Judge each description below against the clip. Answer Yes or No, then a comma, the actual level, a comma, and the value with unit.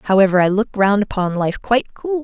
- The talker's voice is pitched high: Yes, high, 210 Hz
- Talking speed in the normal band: No, fast, 215 wpm